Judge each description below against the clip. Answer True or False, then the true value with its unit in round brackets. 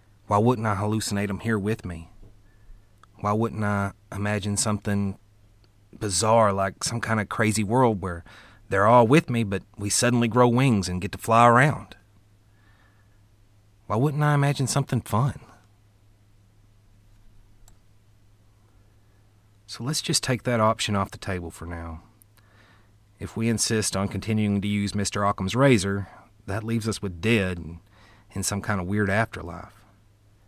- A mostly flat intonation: True (1.6 semitones)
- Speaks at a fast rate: False (145 wpm)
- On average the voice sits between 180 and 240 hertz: False (105 Hz)